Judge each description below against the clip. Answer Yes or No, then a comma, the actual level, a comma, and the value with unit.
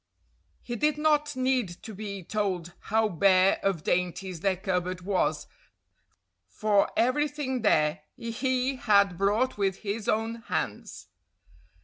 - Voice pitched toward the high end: Yes, high, 205 Hz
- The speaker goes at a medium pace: No, slow, 120 wpm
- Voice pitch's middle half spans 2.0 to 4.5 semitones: No, average, 5.1 semitones